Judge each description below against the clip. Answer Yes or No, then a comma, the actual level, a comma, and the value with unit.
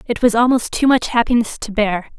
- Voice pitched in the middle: No, high, 230 Hz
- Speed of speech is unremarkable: No, fast, 220 wpm